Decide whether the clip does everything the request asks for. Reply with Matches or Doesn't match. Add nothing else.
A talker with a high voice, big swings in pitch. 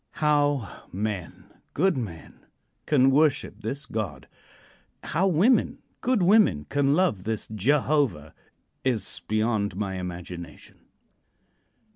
Doesn't match